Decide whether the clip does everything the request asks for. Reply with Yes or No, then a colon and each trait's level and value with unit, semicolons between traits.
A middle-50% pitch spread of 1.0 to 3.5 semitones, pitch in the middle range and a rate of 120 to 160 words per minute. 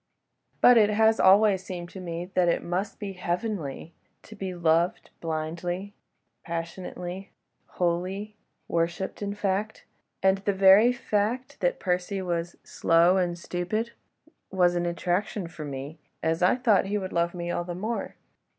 Yes: average, 2.9 semitones; medium, 180 Hz; average, 145 wpm